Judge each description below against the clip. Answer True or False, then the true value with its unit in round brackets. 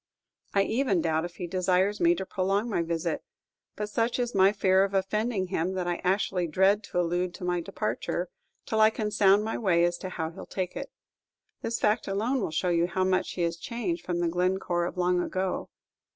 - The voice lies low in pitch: False (185 Hz)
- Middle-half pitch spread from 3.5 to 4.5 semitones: False (2.7 semitones)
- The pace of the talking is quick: True (215 wpm)